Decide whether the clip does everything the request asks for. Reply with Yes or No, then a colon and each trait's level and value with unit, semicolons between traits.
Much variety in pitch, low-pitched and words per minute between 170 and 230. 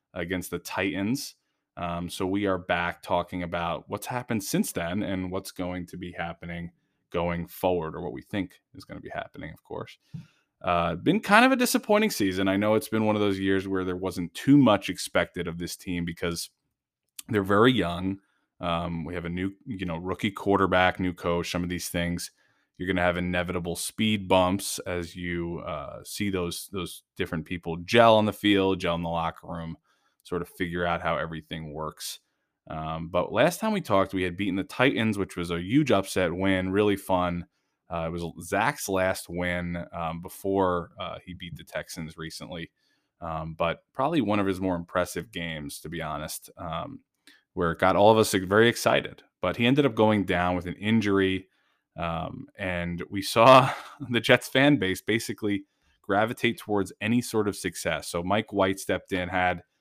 No: average, 2.8 semitones; very low, 90 Hz; average, 190 wpm